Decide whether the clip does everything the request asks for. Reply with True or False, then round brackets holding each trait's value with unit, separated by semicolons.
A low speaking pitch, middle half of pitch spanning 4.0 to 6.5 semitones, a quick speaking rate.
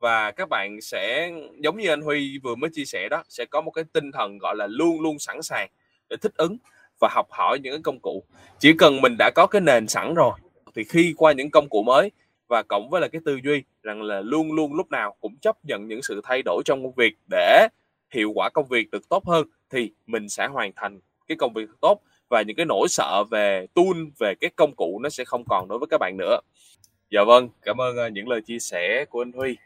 False (145 Hz; 5.6 semitones; 245 wpm)